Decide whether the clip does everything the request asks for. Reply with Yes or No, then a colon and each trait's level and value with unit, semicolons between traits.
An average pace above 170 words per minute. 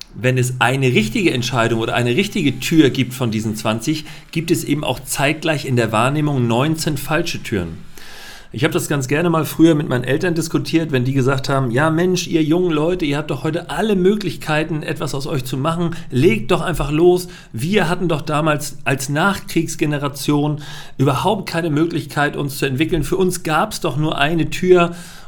Yes: fast, 190 wpm